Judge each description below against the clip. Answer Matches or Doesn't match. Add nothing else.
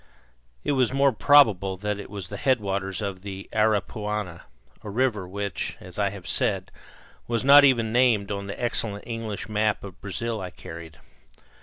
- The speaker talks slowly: Doesn't match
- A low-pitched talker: Matches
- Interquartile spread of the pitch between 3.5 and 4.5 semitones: Doesn't match